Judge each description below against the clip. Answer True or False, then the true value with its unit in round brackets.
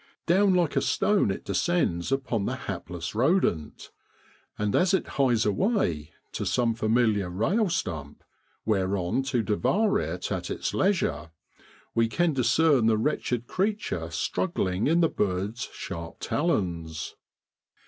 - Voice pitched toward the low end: True (115 Hz)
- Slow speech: True (130 wpm)